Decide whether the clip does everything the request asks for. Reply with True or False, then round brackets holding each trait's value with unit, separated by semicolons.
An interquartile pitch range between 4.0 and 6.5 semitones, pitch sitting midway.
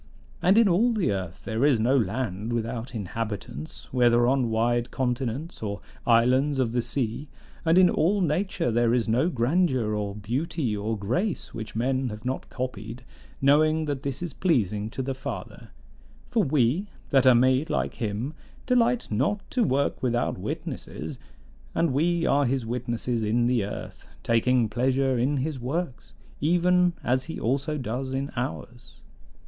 False (4.4 semitones; 125 Hz)